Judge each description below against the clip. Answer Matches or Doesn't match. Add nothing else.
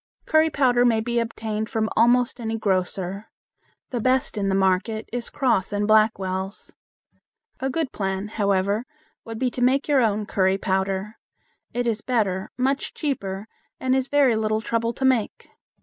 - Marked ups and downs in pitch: Doesn't match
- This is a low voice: Doesn't match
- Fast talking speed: Doesn't match